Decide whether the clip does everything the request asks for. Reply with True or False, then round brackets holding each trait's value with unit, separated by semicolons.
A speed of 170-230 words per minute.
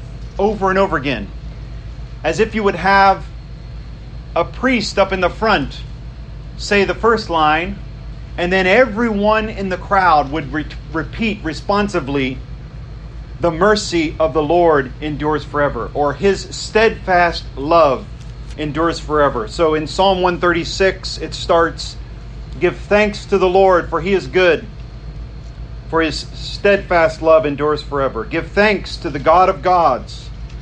False (135 wpm)